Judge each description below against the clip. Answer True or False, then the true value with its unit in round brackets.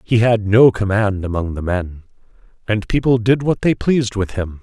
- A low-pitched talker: True (105 Hz)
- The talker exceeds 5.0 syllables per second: False (4.9 syllables/s)